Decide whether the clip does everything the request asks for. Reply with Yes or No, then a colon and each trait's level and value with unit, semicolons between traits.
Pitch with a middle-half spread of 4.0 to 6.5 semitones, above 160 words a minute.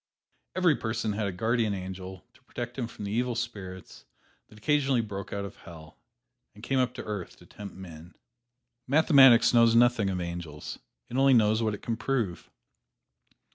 Yes: average, 4.3 semitones; average, 175 wpm